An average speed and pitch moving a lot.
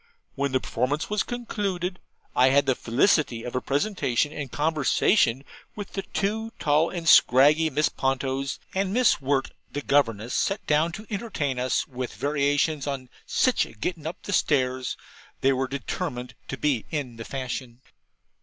No: average, 155 wpm; average, 4.7 semitones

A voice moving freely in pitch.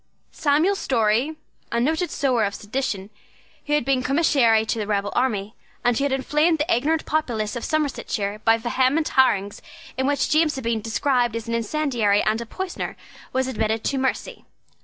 No: average, 4.8 semitones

